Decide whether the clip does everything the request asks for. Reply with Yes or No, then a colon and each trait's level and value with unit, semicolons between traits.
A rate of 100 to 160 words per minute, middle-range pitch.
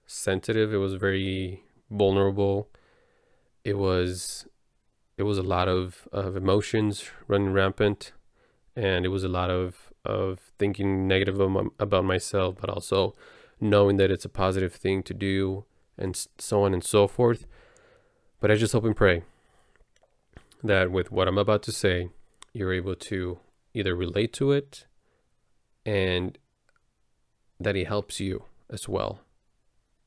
No: average, 140 wpm; very low, 95 Hz